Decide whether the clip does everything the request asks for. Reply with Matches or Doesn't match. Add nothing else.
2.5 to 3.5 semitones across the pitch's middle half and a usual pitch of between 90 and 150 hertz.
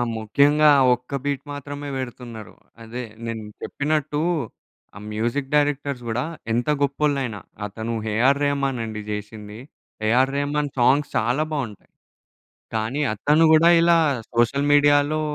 Doesn't match